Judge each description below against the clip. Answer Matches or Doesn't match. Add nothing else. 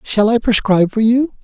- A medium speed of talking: Doesn't match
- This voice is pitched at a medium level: Doesn't match